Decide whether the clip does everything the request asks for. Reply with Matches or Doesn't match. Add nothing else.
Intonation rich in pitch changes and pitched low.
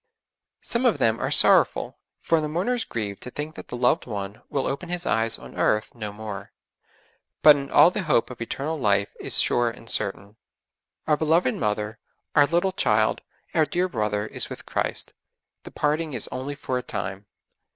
Matches